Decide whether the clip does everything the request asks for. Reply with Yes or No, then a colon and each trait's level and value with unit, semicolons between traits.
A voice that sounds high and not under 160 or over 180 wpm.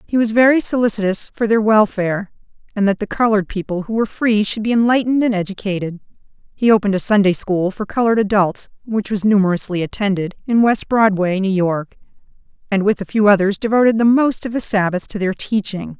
No: high, 205 Hz; average, 190 wpm